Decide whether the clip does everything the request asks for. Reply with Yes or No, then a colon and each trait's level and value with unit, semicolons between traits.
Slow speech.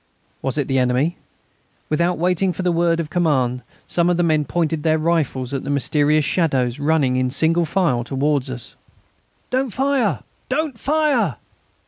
No: average, 160 wpm